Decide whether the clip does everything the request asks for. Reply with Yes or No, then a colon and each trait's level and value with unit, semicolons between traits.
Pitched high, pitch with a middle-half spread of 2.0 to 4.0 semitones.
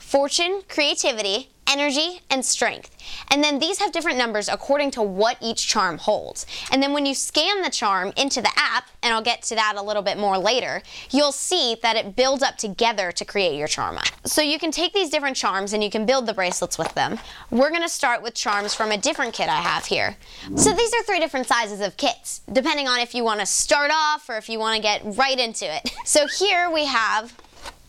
No: very high, 255 Hz; wide, 5.5 semitones